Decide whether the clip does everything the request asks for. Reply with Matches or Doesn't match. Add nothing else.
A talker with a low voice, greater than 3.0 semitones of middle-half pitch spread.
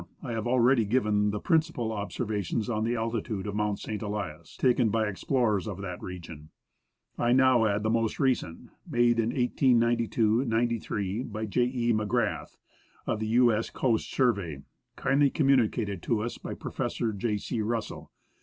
Doesn't match